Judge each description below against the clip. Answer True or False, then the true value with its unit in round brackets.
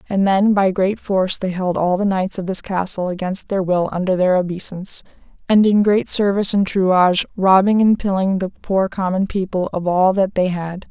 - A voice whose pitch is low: False (190 Hz)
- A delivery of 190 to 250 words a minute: True (205 wpm)